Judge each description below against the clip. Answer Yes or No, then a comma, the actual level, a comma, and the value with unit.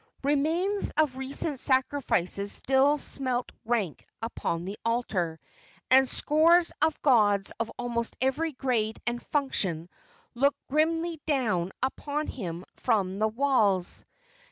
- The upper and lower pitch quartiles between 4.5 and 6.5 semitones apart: Yes, wide, 5.5 semitones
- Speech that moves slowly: Yes, slow, 115 wpm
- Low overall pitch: No, very high, 255 Hz